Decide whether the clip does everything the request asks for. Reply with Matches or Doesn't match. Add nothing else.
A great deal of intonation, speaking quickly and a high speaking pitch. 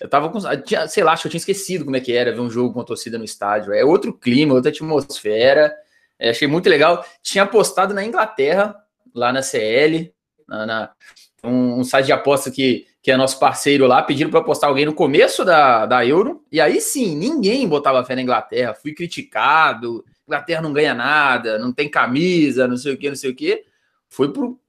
Doesn't match